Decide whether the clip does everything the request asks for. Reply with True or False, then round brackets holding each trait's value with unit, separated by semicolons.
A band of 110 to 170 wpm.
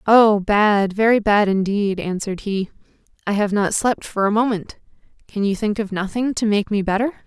False (190 wpm)